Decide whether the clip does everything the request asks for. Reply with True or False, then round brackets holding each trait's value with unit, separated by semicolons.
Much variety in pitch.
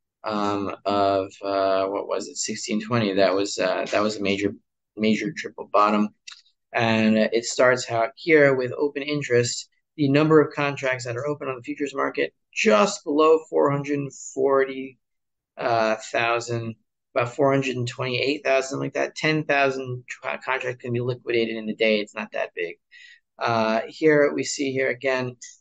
False (4.4 semitones)